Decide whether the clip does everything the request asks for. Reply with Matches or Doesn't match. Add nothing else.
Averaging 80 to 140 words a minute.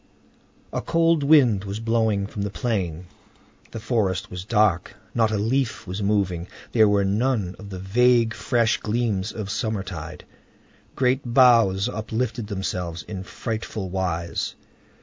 Matches